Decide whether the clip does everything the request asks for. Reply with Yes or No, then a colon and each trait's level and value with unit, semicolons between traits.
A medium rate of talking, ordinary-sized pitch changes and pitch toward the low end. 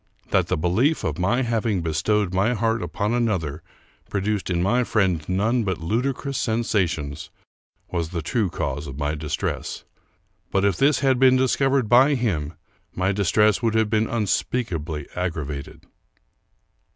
No: average, 150 wpm; wide, 5.9 semitones; low, 100 Hz